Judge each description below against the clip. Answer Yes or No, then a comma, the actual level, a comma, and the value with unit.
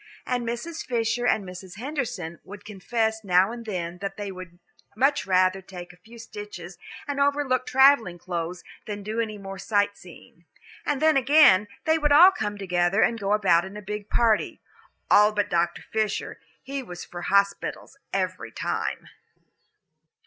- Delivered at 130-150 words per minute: No, average, 165 wpm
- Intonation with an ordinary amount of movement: Yes, average, 4.4 semitones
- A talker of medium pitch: No, high, 205 Hz